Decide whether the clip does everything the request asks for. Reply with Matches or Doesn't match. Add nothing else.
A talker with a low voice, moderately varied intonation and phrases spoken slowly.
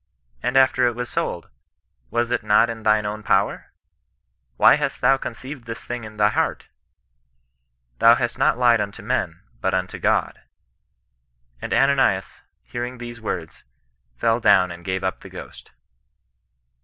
Doesn't match